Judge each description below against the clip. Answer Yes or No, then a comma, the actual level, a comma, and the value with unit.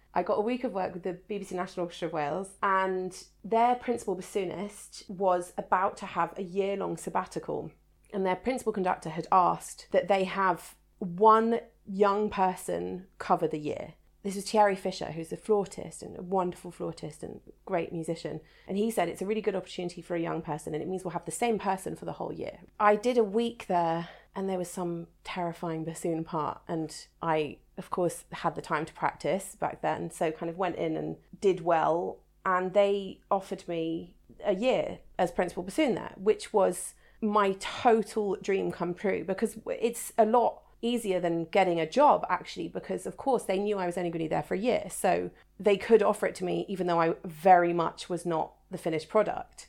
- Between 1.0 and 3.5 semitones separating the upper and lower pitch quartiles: Yes, average, 3.2 semitones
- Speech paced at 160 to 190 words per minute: No, average, 200 wpm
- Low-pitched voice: No, medium, 185 Hz